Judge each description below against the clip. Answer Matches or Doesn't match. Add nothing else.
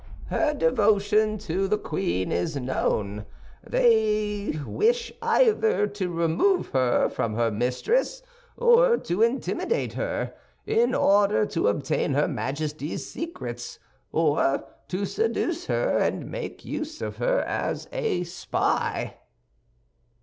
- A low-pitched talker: Doesn't match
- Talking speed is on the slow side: Matches